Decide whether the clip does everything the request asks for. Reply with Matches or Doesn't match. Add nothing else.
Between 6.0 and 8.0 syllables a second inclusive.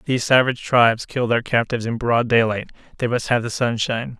Matches